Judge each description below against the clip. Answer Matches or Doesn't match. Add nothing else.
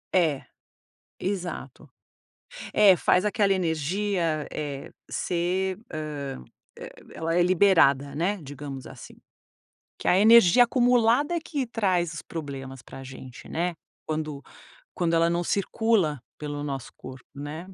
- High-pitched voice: Doesn't match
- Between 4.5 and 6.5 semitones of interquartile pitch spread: Matches